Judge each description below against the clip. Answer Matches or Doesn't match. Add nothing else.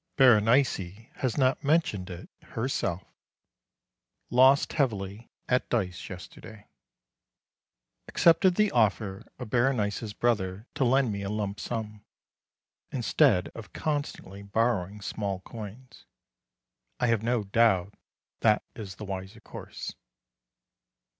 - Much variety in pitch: Doesn't match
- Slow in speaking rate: Matches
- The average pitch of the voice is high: Doesn't match